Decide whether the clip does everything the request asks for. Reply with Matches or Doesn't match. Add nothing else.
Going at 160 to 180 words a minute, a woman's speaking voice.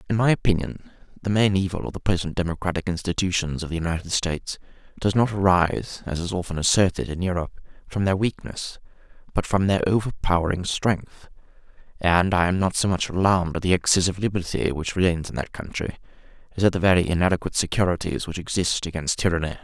Doesn't match